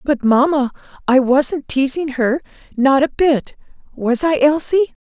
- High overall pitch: Yes, very high, 280 Hz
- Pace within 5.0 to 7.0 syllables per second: No, 4.0 syllables/s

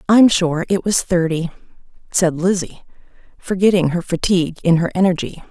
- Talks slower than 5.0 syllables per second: No, 5.1 syllables/s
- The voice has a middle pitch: Yes, medium, 180 Hz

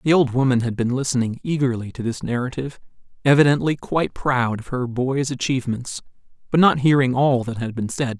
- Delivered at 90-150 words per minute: No, average, 185 wpm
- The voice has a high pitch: No, low, 130 Hz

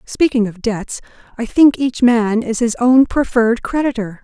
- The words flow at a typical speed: Yes, average, 170 wpm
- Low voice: No, high, 235 Hz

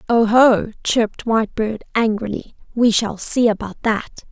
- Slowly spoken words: Yes, slow, 125 wpm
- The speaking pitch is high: Yes, high, 220 Hz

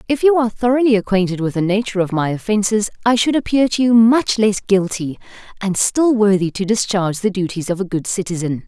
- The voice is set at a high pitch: Yes, high, 205 Hz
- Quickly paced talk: Yes, fast, 210 wpm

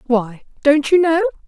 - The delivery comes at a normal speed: Yes, average, 160 wpm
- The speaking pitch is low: No, very high, 290 Hz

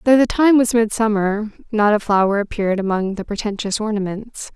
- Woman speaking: Yes, female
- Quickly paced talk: No, average, 170 wpm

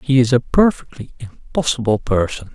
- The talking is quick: No, average, 140 wpm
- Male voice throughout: Yes, male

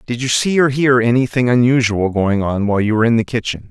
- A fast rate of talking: Yes, fast, 245 wpm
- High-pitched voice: No, low, 120 Hz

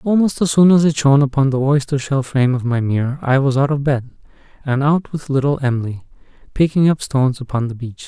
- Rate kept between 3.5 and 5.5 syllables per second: No, 5.9 syllables/s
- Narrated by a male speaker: Yes, male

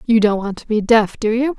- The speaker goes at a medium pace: No, fast, 300 wpm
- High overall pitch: Yes, high, 220 Hz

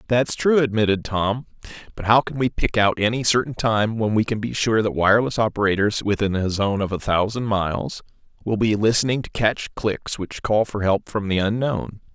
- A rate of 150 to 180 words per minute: No, fast, 205 wpm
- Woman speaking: No, male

